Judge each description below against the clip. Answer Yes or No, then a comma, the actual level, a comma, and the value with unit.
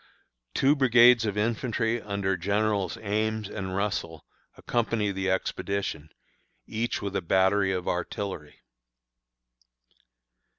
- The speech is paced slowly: Yes, slow, 100 wpm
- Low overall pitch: Yes, low, 100 Hz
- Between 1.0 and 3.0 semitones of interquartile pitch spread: Yes, narrow, 2.6 semitones